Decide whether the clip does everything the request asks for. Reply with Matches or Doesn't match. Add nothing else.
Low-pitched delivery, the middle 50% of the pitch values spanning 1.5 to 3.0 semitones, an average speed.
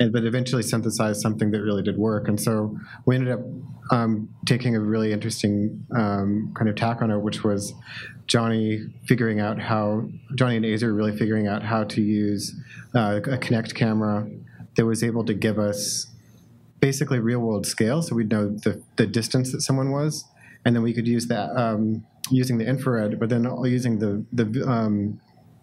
Matches